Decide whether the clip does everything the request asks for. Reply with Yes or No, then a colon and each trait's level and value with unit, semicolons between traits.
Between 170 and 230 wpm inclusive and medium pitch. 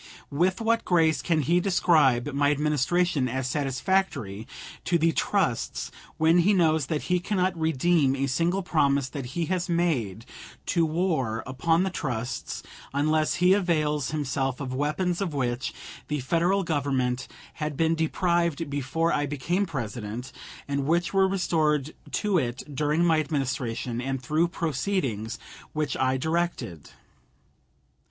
No: average, 140 wpm; medium, 155 Hz